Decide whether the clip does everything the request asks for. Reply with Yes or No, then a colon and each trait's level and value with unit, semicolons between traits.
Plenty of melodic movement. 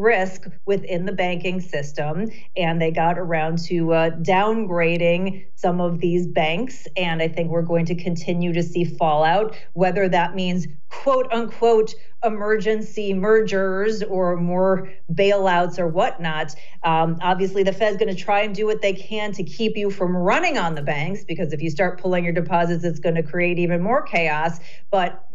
No: average, 3.1 semitones